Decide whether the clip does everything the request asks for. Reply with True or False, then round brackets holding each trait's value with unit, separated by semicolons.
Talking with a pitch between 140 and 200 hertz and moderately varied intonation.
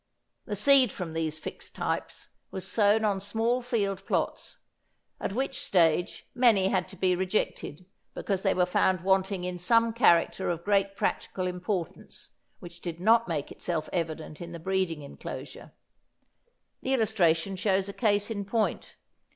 True (190 Hz; 3.3 semitones)